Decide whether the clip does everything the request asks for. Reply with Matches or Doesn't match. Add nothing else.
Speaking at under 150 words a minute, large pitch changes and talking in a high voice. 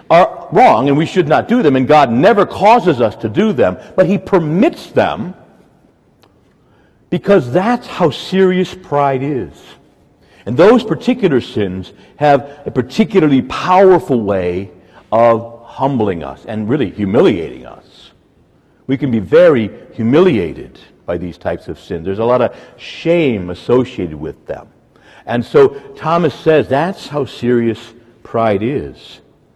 Doesn't match